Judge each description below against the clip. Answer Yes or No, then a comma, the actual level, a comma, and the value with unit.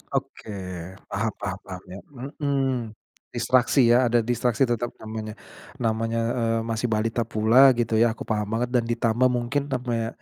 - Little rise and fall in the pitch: Yes, narrow, 1.9 semitones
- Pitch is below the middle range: Yes, low, 115 Hz